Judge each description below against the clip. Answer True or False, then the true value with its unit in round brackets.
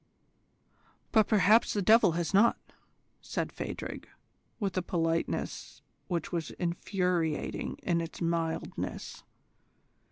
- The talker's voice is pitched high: False (175 Hz)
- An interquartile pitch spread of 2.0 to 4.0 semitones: True (3.1 semitones)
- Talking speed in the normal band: False (100 wpm)